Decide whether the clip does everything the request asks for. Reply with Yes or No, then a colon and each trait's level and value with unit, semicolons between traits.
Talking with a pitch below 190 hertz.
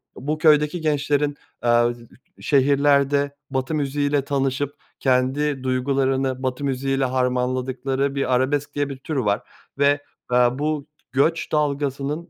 Yes: medium, 140 Hz